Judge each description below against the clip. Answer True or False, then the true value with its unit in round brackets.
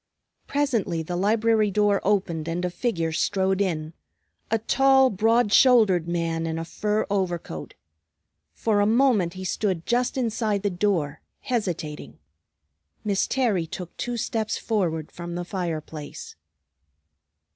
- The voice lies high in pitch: True (195 Hz)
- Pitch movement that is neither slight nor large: True (4.6 semitones)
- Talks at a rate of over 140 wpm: False (135 wpm)